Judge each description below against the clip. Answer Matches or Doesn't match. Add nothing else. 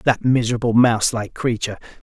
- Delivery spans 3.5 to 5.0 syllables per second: Doesn't match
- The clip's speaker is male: Matches